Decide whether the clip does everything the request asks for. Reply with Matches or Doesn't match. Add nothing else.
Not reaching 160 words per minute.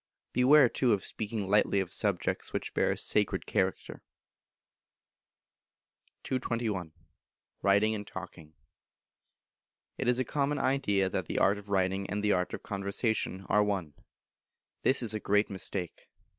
Matches